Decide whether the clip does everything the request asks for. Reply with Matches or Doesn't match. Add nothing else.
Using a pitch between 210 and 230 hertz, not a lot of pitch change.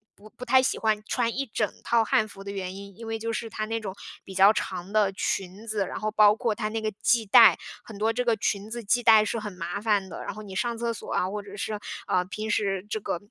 Matches